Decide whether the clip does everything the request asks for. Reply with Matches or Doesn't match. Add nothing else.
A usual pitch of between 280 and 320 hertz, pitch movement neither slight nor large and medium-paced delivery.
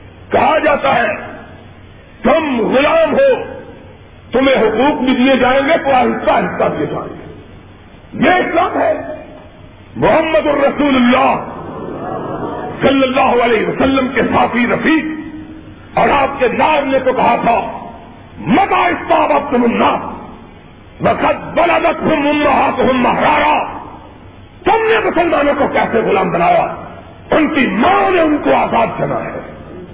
Matches